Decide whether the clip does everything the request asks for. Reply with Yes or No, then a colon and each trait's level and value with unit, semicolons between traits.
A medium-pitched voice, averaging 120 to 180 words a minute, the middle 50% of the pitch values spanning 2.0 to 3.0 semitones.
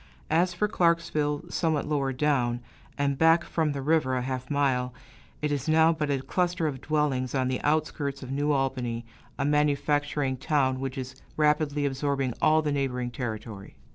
Yes: medium, 145 Hz; average, 170 wpm; narrow, 2.6 semitones